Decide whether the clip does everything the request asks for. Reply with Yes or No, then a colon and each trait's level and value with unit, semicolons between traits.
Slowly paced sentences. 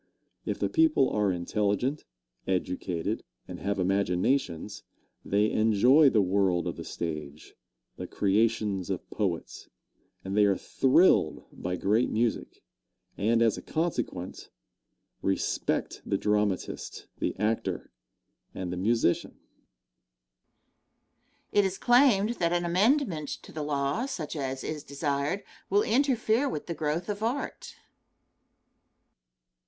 Yes: slow, 120 wpm